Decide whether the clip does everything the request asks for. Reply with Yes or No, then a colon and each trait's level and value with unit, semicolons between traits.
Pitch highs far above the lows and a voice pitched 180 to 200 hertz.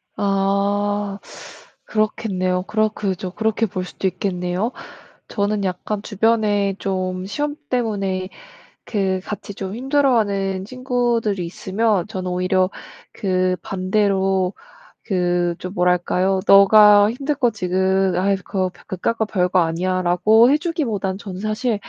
No: narrow, 2.6 semitones; high, 195 Hz